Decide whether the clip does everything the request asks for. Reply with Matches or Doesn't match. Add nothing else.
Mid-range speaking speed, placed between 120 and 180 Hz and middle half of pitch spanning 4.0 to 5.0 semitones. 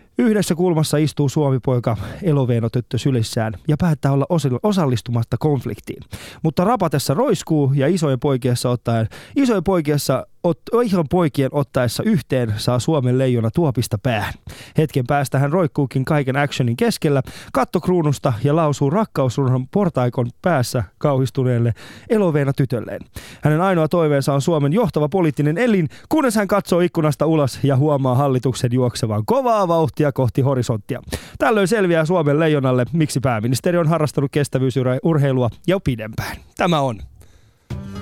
Matches